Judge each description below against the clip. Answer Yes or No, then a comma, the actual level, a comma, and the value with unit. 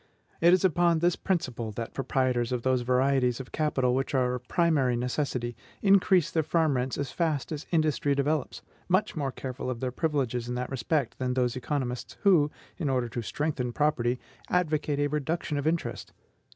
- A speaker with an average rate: Yes, average, 180 wpm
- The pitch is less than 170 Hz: Yes, low, 135 Hz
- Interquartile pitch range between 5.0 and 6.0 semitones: No, average, 4.0 semitones